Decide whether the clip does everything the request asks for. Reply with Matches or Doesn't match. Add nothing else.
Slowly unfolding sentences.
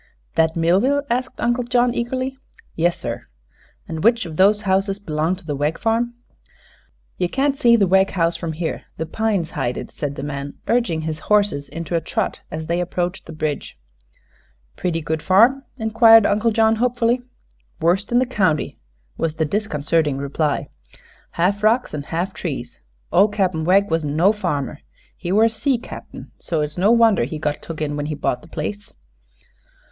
Doesn't match